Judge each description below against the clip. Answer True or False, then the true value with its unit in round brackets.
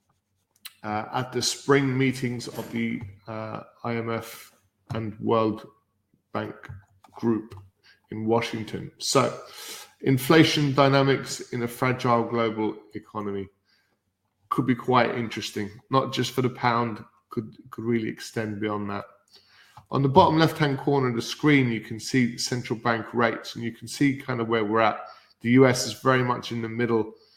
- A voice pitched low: True (115 Hz)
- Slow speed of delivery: False (155 wpm)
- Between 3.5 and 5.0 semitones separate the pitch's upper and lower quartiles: False (2.9 semitones)